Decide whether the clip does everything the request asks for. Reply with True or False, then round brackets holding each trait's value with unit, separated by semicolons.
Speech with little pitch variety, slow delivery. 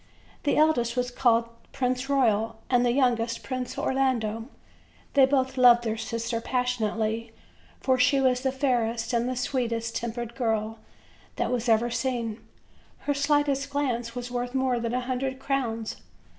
False (2.3 semitones; 155 wpm)